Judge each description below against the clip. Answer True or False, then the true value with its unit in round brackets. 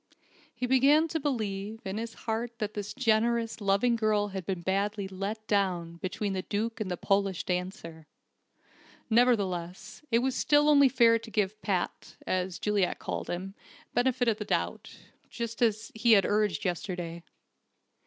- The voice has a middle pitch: False (210 Hz)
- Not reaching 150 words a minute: False (160 wpm)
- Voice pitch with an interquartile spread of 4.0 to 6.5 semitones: False (3.4 semitones)